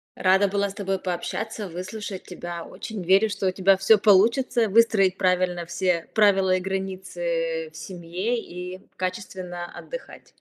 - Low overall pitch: No, high, 190 Hz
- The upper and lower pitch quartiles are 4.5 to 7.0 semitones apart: No, average, 2.9 semitones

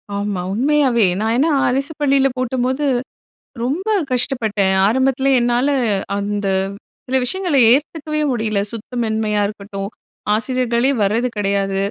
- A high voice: Yes, high, 240 Hz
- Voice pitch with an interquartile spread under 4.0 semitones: No, average, 4.5 semitones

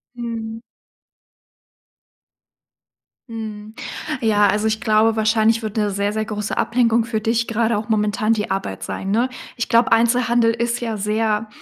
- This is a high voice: Yes, high, 220 Hz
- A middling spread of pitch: No, narrow, 1.4 semitones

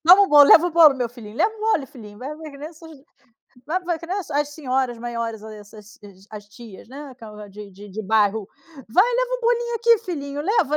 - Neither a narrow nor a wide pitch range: No, wide, 7.8 semitones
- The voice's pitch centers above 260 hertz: Yes, very high, 280 Hz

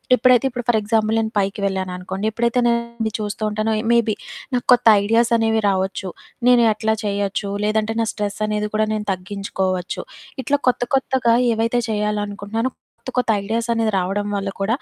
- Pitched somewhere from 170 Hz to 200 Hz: No, high, 215 Hz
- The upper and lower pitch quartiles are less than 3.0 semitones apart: Yes, narrow, 2.4 semitones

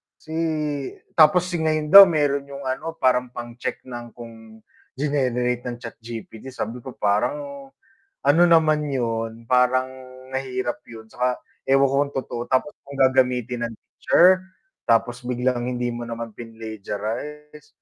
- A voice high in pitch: No, low, 125 Hz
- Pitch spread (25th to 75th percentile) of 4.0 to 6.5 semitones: No, average, 3.6 semitones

